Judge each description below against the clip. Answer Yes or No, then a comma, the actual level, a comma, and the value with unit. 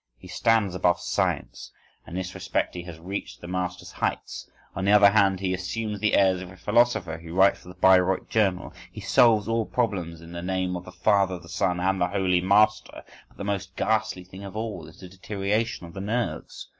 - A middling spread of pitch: No, narrow, 2.3 semitones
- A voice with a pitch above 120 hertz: No, very low, 95 Hz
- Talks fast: Yes, fast, 215 wpm